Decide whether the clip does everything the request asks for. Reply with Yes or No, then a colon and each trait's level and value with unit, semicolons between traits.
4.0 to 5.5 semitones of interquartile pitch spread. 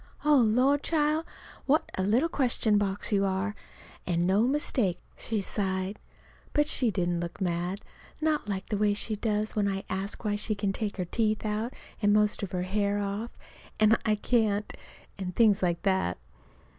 No: average, 2.8 semitones